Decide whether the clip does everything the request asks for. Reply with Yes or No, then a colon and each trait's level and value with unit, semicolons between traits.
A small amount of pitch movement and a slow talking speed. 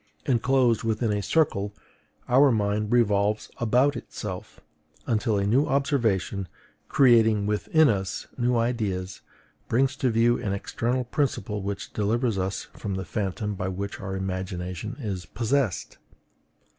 No: average, 3.7 semitones; slow, 130 wpm